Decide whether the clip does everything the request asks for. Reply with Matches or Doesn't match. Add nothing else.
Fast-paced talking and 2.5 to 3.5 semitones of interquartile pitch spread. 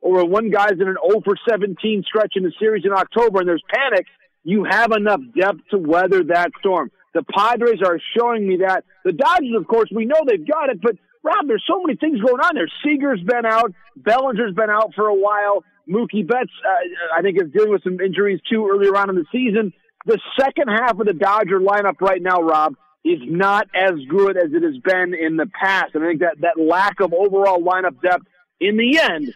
Doesn't match